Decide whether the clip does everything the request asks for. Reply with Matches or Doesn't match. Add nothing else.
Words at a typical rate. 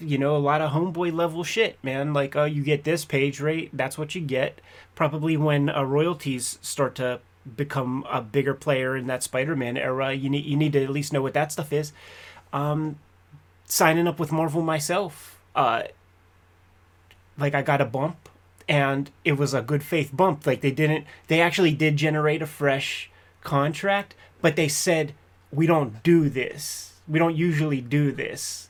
Matches